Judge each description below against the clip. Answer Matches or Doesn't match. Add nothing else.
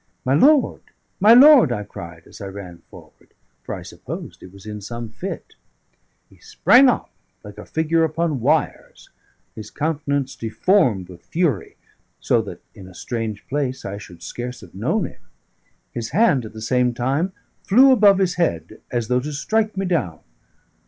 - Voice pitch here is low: Matches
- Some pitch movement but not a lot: Doesn't match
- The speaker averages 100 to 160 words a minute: Doesn't match